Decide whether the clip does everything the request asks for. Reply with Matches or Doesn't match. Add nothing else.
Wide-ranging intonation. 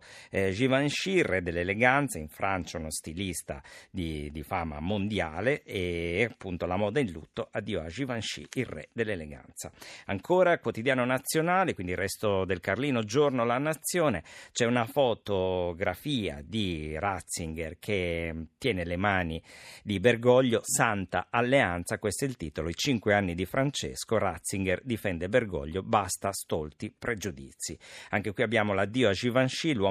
Matches